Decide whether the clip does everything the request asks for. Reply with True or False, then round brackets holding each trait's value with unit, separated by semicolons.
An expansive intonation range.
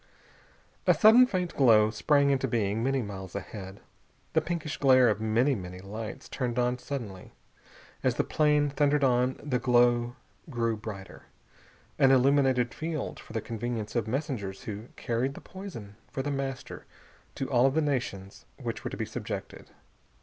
False (4.4 semitones)